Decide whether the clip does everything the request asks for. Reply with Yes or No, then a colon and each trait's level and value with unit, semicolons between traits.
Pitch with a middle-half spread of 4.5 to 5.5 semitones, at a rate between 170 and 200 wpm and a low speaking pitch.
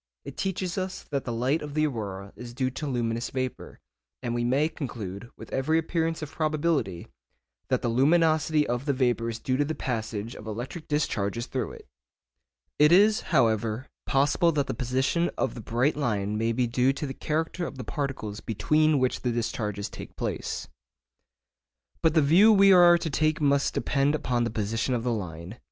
Yes: average, 4.9 semitones; average, 185 wpm; low, 130 Hz